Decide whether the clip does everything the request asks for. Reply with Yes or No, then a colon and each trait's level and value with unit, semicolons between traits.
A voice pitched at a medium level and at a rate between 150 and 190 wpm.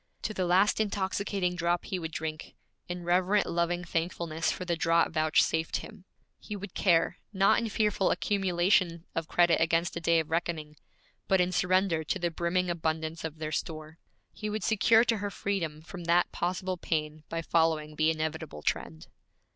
Yes: medium, 170 Hz; average, 170 wpm